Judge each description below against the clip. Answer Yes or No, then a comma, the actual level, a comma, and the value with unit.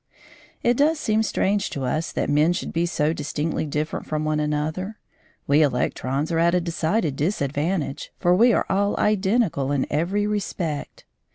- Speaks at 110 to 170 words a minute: Yes, average, 165 wpm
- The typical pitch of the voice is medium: Yes, medium, 165 Hz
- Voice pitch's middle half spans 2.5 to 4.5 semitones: No, average, 5.1 semitones